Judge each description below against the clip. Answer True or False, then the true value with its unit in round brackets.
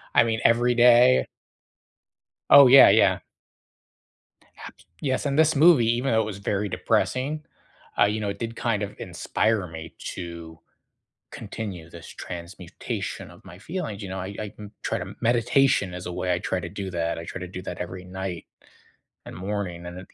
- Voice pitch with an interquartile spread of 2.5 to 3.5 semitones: False (4.9 semitones)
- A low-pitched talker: True (100 Hz)